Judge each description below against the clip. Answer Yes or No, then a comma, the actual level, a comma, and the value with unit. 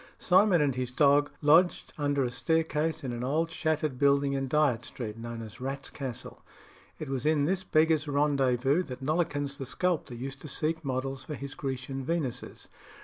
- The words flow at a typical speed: Yes, average, 175 wpm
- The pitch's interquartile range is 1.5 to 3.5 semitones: Yes, average, 3.1 semitones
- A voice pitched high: No, medium, 140 Hz